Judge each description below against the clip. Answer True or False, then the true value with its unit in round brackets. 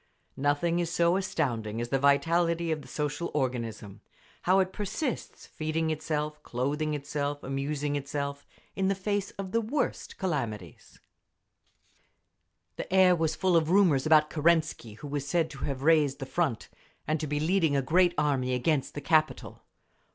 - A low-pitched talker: False (150 Hz)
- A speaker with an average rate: True (155 wpm)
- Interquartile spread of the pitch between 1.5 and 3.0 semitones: False (3.5 semitones)